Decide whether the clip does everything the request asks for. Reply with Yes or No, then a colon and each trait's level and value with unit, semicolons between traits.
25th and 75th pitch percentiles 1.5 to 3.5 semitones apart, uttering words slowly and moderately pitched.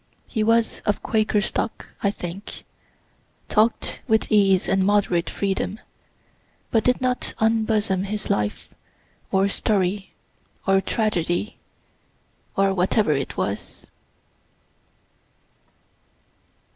No: narrow, 2.4 semitones; slow, 95 wpm; high, 200 Hz